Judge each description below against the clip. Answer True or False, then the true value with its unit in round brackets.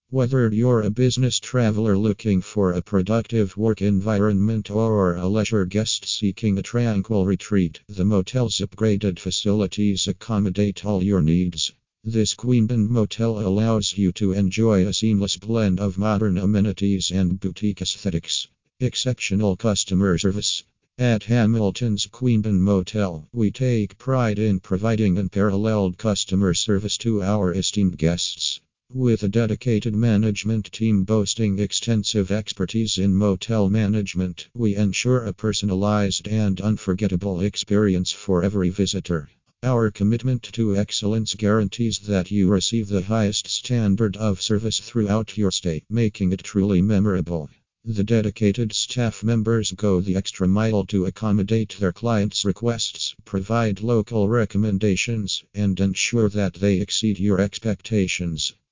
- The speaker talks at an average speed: False (130 wpm)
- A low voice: True (105 Hz)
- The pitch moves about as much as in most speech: False (2.3 semitones)